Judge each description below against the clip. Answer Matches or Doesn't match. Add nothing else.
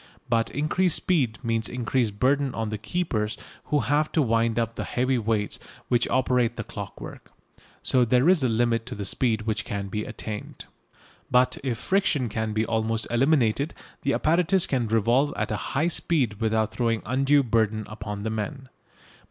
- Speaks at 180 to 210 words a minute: Doesn't match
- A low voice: Matches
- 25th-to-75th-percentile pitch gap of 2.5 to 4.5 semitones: Matches